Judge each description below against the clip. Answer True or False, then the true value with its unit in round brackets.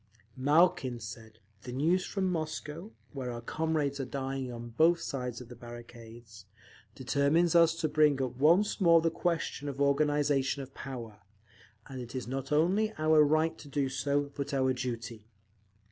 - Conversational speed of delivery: True (165 wpm)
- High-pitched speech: False (140 Hz)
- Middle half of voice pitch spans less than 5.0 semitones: True (4.0 semitones)